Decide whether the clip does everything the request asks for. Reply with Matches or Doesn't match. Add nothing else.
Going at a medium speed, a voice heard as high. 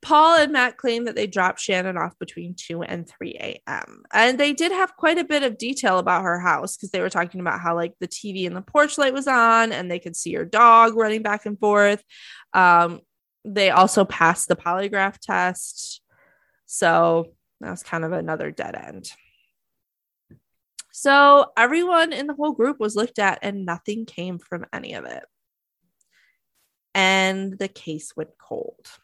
Matches